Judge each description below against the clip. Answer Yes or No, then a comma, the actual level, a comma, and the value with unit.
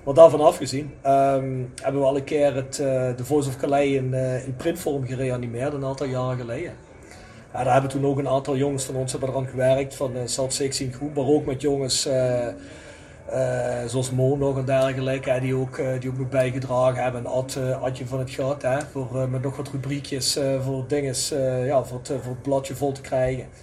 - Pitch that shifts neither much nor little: No, narrow, 1.4 semitones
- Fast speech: Yes, fast, 215 wpm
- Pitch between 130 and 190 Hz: Yes, low, 135 Hz